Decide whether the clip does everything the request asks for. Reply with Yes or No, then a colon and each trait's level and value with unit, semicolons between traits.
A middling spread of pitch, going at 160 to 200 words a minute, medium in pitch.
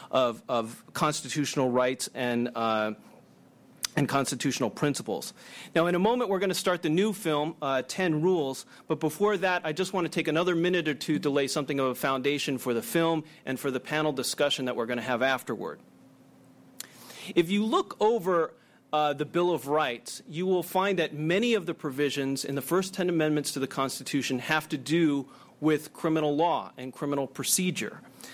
Yes: average, 4.3 semitones; average, 190 wpm; medium, 150 Hz